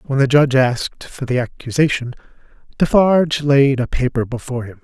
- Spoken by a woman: No, male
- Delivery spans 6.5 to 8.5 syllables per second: No, 5.6 syllables/s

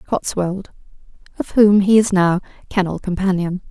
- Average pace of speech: No, slow, 130 wpm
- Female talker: Yes, female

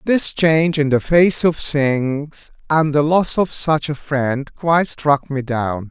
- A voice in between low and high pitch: Yes, medium, 150 Hz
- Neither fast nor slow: Yes, average, 185 wpm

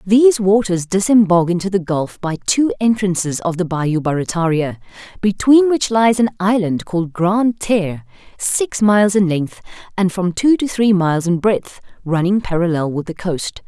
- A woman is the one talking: Yes, female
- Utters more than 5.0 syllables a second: No, 4.8 syllables/s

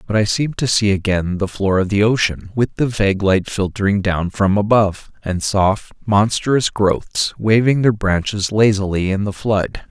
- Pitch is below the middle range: Yes, low, 100 Hz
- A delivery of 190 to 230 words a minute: No, average, 180 wpm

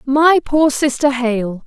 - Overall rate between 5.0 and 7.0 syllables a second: No, 3.3 syllables/s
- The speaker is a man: No, female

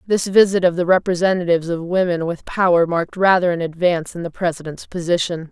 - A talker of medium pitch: Yes, medium, 175 Hz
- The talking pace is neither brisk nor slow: Yes, average, 185 wpm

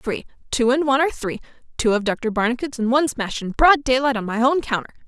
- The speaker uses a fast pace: Yes, fast, 215 wpm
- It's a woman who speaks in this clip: Yes, female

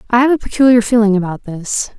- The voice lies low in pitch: No, high, 225 Hz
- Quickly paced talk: Yes, fast, 210 wpm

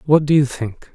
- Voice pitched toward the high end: No, low, 135 Hz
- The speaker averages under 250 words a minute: No, fast, 255 wpm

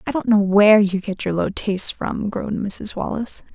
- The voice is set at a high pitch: Yes, high, 205 Hz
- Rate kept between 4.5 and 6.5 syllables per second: Yes, 5.4 syllables/s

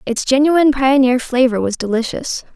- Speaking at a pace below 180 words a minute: Yes, average, 140 wpm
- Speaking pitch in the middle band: No, very high, 260 Hz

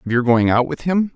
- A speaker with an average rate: No, fast, 310 wpm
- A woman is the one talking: No, male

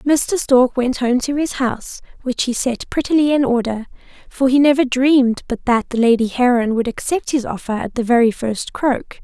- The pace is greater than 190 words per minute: Yes, average, 200 wpm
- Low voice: No, very high, 250 Hz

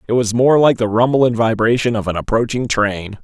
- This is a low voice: Yes, low, 115 Hz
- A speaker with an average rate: No, fast, 220 wpm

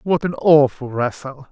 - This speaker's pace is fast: No, average, 160 wpm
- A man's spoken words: Yes, male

